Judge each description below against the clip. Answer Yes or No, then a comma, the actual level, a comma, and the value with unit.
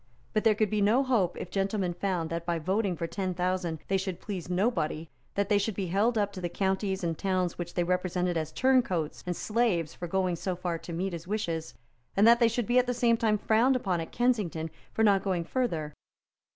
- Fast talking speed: Yes, fast, 225 wpm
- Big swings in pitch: No, average, 3.7 semitones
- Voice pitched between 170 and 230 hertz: Yes, high, 190 Hz